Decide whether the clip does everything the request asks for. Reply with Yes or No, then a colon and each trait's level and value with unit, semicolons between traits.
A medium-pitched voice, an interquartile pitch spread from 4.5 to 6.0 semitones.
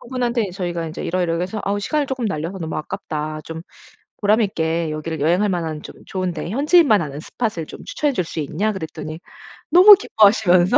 Yes: medium, 180 Hz; average, 5.1 semitones